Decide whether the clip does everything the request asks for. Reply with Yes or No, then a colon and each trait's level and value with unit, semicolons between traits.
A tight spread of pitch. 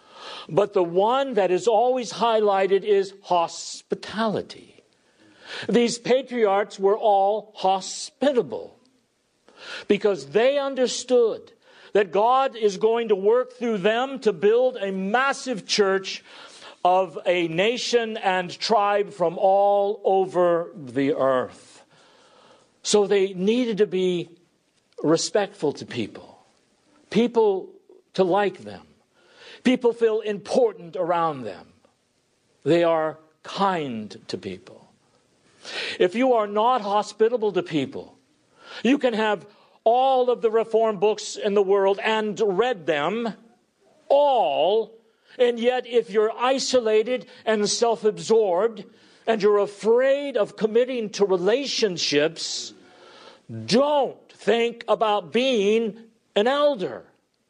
No: average, 4.1 semitones